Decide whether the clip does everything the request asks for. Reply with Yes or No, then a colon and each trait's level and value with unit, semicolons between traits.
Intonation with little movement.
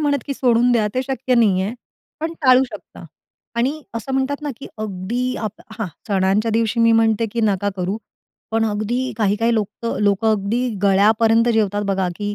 No: average, 3.2 semitones